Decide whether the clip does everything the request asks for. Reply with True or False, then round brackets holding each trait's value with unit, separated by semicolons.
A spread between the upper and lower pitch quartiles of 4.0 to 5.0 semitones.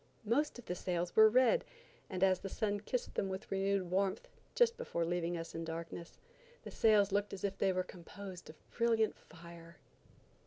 False (3.3 semitones)